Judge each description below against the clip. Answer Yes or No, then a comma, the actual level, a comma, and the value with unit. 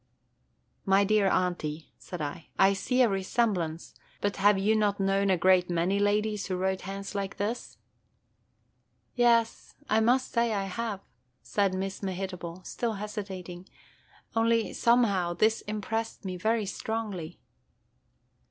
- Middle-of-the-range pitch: No, high, 200 Hz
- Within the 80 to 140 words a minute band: Yes, slow, 135 wpm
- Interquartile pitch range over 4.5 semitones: No, average, 2.8 semitones